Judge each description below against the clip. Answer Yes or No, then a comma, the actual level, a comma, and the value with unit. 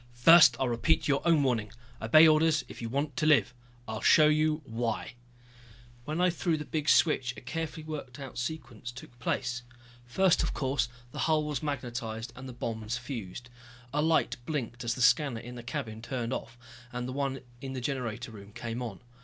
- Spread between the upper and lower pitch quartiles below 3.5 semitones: No, average, 4.2 semitones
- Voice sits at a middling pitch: No, low, 125 Hz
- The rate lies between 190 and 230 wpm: Yes, average, 195 wpm